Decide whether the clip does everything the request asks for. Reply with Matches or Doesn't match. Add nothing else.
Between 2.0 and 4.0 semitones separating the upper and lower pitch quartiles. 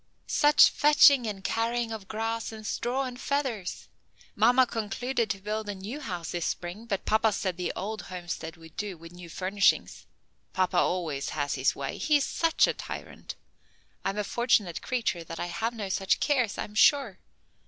Doesn't match